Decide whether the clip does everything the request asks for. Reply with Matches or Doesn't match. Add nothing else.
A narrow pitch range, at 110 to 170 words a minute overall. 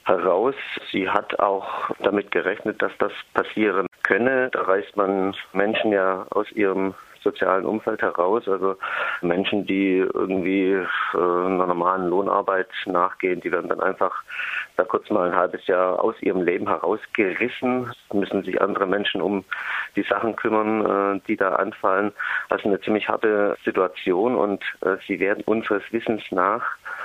Matches